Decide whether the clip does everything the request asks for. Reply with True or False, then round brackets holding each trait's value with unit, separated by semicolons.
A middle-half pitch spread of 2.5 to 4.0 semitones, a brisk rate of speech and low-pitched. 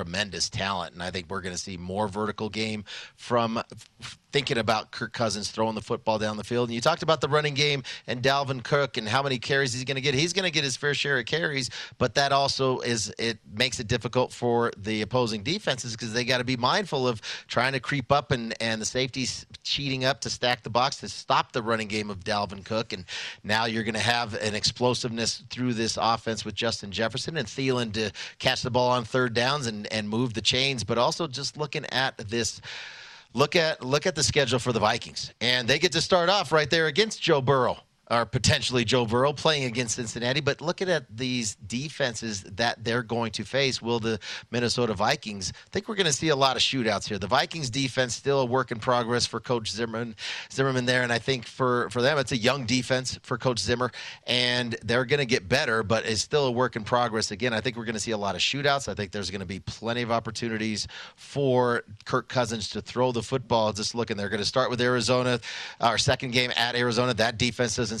True (2.9 semitones; 225 wpm; 120 Hz)